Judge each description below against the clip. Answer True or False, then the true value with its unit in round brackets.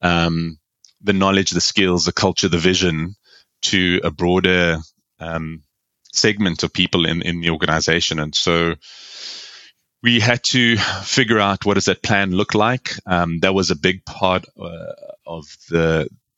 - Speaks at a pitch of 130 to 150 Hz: False (90 Hz)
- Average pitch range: True (3.0 semitones)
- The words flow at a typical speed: True (155 wpm)